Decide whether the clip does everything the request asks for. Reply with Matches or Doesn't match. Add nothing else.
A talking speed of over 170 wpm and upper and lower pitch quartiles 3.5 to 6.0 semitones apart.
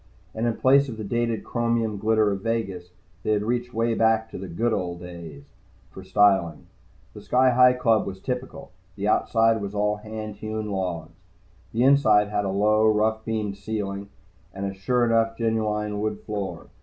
Doesn't match